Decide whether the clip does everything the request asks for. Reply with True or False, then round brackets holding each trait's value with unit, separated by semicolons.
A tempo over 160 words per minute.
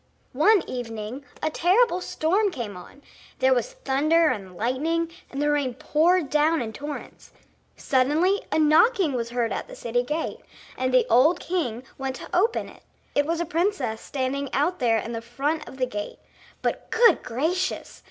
True (170 wpm)